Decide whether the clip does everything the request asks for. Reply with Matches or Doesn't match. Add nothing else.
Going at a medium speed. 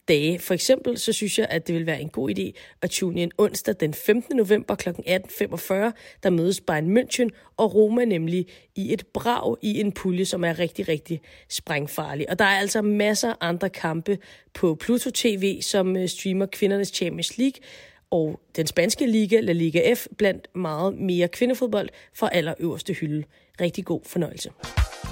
Matches